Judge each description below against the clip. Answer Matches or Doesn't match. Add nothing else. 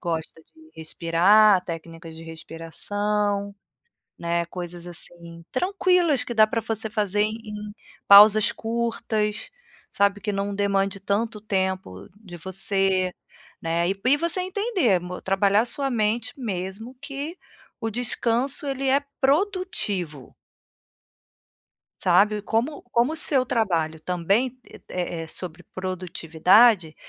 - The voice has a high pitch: Matches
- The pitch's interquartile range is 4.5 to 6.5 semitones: Matches